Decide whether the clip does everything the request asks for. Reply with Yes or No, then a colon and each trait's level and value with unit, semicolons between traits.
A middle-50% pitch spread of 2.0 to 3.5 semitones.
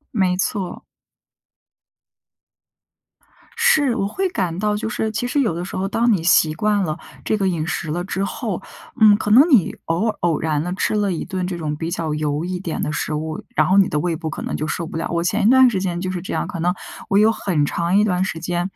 No: average, 4.1 semitones